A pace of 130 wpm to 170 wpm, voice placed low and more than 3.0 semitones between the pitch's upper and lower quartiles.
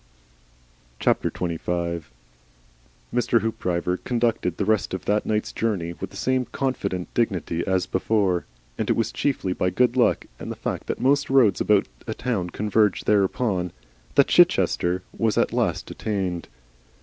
Yes: average, 145 wpm; low, 100 Hz; average, 4.1 semitones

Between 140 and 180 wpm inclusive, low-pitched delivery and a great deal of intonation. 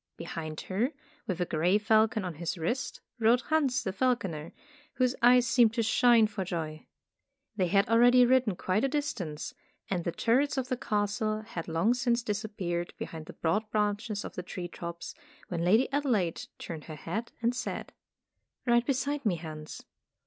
No: average, 175 wpm; high, 215 Hz; wide, 5.7 semitones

